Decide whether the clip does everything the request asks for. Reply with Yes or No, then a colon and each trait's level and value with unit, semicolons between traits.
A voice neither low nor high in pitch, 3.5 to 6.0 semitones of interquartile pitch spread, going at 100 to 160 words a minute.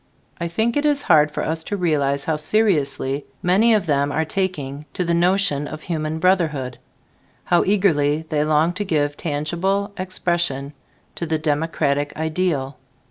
Yes: medium, 160 Hz; average, 3.9 semitones; average, 155 wpm